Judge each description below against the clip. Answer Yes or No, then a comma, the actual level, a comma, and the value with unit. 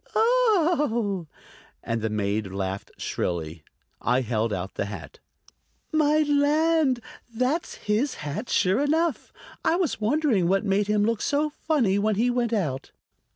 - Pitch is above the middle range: Yes, high, 215 Hz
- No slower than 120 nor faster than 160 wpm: Yes, average, 140 wpm